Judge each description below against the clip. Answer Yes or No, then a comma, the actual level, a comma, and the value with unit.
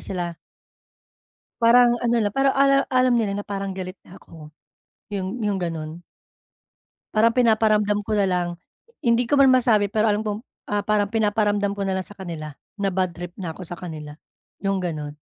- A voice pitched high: Yes, high, 205 Hz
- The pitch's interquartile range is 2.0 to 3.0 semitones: No, average, 3.8 semitones